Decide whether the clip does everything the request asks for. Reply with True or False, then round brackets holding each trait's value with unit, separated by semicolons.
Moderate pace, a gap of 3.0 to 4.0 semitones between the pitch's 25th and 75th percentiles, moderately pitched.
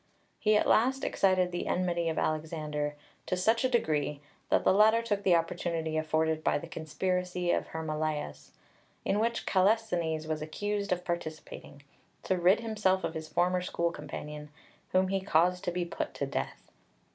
True (165 wpm; 3.4 semitones; 175 Hz)